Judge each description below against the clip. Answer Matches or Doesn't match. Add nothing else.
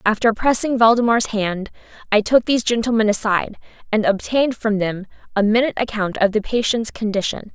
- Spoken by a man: Doesn't match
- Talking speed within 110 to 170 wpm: Matches